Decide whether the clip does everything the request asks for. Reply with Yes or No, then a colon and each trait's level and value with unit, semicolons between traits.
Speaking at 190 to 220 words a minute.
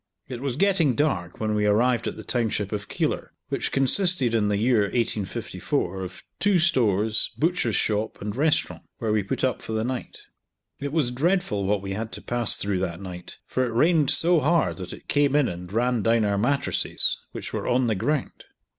Yes: average, 200 wpm